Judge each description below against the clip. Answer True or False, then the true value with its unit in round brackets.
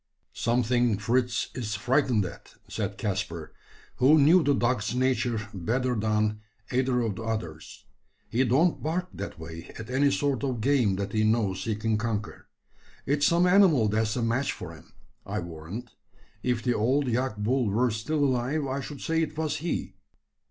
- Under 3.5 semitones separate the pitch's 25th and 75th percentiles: False (4.2 semitones)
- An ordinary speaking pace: True (170 wpm)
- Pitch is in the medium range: False (120 Hz)